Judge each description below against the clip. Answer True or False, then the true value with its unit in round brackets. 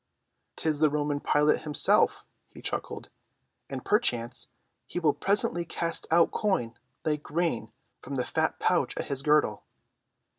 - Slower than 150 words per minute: True (140 wpm)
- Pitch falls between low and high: True (150 Hz)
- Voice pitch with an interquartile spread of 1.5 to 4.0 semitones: True (3.2 semitones)